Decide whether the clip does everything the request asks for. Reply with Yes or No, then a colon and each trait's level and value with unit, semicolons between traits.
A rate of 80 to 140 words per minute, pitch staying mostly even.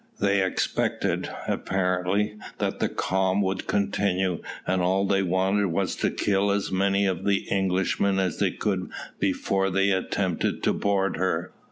No: average, 150 wpm; narrow, 1.2 semitones